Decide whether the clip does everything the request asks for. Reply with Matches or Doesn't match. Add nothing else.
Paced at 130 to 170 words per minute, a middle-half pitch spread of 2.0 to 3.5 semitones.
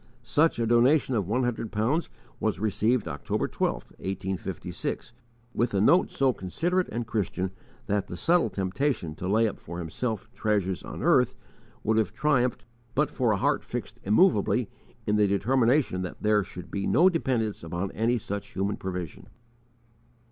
Doesn't match